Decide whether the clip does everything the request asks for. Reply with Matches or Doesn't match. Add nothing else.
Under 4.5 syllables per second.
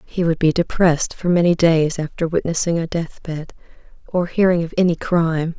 Doesn't match